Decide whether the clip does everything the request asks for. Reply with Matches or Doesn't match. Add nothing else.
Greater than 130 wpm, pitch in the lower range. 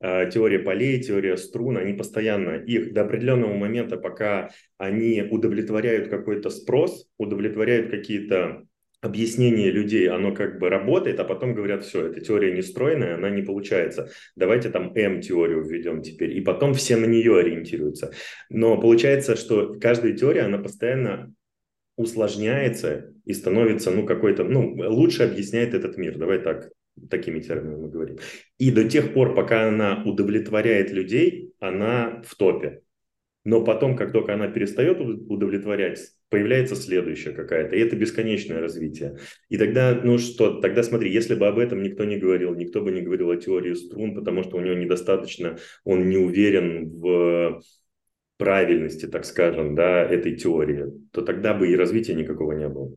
Matches